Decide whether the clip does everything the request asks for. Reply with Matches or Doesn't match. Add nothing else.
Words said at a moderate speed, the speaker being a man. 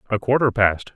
Matches